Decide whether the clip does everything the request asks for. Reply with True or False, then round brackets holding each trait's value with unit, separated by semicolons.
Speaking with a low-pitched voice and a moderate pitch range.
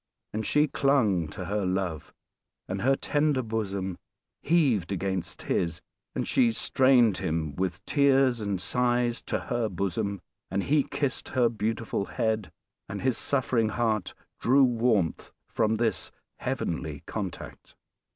True (110 Hz; 4.9 semitones)